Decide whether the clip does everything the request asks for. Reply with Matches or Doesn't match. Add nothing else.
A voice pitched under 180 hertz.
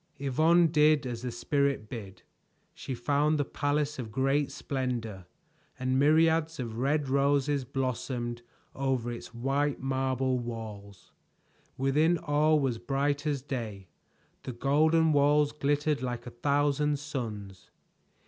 Matches